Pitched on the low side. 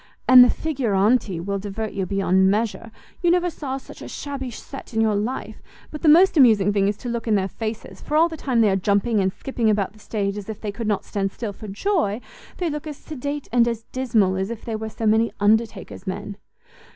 No: high, 220 Hz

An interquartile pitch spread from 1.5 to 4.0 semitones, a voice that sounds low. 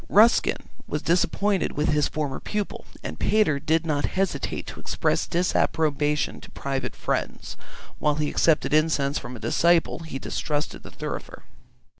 No: average, 2.9 semitones; medium, 155 Hz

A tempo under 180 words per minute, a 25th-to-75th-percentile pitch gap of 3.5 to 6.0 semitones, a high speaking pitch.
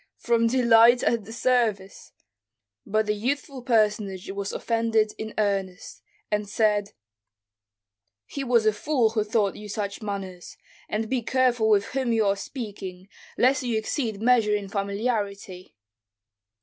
No: slow, 135 wpm; average, 2.8 semitones; high, 215 Hz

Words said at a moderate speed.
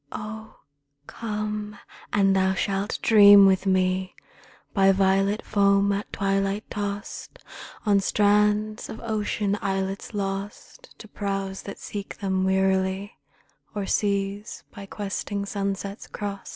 No: slow, 115 wpm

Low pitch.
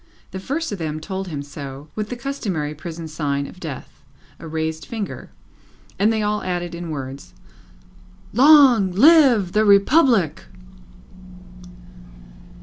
No: medium, 185 Hz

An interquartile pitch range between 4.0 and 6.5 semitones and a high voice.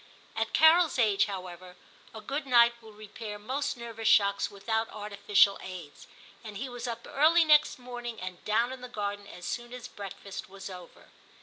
No: average, 3.6 semitones; high, 220 Hz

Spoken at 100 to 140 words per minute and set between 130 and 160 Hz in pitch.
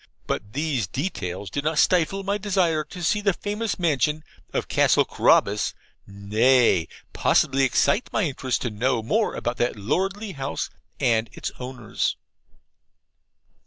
Yes: slow, 135 wpm; medium, 140 Hz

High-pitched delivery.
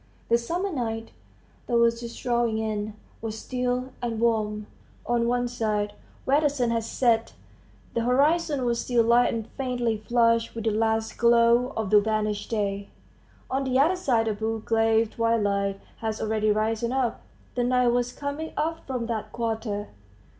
Yes: high, 230 Hz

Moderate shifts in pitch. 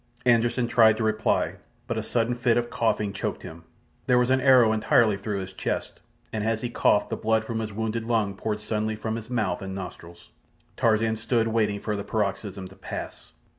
No: narrow, 1.9 semitones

